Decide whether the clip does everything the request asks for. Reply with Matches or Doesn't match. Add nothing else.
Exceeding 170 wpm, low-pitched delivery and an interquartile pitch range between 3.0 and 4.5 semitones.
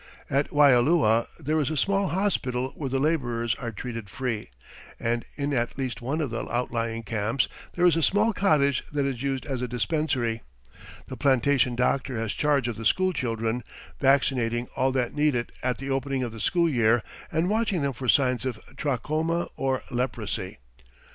Matches